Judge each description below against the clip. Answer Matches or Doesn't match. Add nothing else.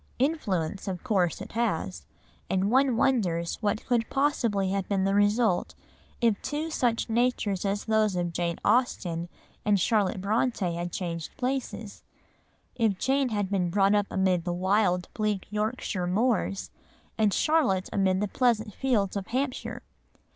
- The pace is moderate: Matches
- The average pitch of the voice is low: Doesn't match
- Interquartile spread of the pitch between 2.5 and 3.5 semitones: Doesn't match